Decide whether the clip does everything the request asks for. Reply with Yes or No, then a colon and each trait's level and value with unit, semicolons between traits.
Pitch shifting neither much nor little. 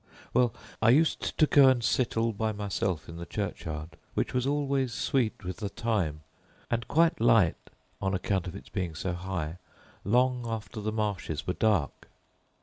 Yes: average, 4.9 semitones